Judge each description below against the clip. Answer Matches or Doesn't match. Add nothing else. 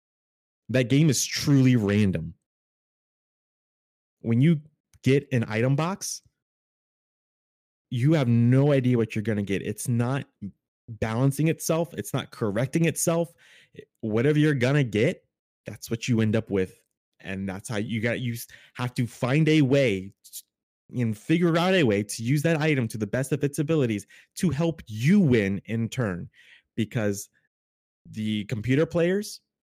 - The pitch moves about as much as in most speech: Doesn't match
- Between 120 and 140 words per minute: Doesn't match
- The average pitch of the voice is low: Matches